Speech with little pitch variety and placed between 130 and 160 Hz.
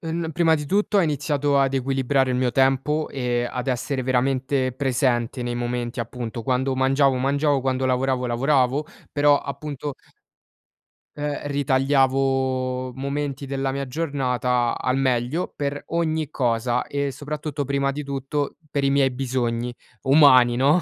Yes: narrow, 2.1 semitones; low, 135 Hz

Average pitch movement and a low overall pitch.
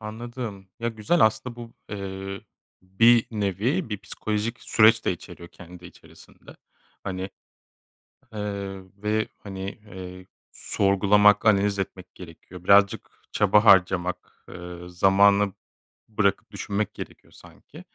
No: narrow, 2.2 semitones; low, 100 Hz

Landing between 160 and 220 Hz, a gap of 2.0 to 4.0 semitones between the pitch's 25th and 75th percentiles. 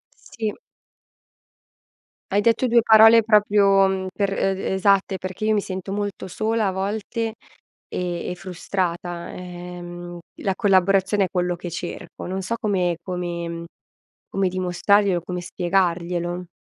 Yes: high, 190 Hz; narrow, 2.4 semitones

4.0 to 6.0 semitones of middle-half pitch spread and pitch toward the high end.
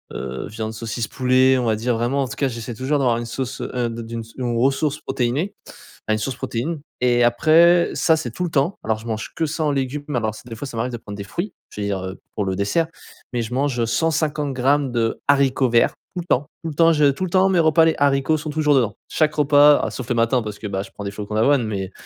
No: average, 4.7 semitones; low, 130 Hz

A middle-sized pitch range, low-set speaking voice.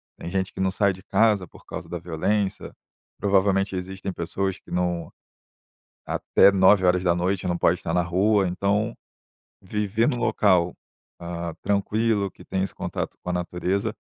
No: narrow, 2.3 semitones; very low, 95 Hz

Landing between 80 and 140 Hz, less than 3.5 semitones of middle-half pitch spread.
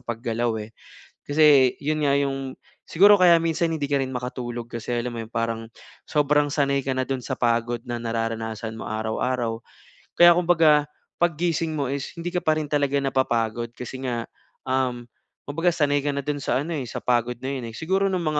No: low, 135 Hz; average, 4.2 semitones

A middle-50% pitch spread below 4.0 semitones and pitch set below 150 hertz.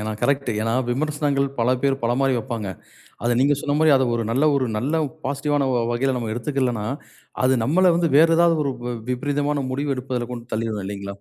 Yes: average, 3.6 semitones; low, 135 Hz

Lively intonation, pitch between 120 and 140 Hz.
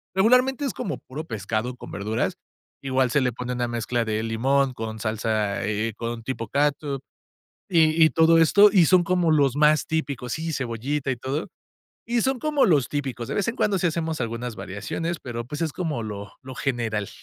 Yes: wide, 5.8 semitones; low, 135 Hz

